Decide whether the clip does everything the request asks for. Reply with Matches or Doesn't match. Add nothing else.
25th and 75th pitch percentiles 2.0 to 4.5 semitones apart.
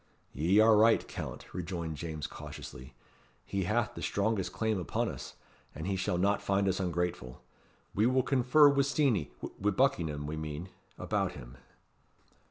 Doesn't match